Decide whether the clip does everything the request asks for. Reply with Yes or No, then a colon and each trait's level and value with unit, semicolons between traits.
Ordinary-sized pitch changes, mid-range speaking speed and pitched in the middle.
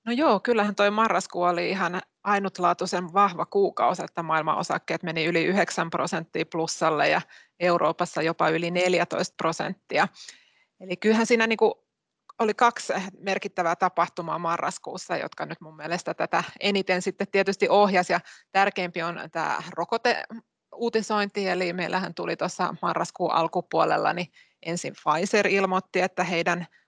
Yes: average, 3.1 semitones; average, 130 wpm; medium, 180 Hz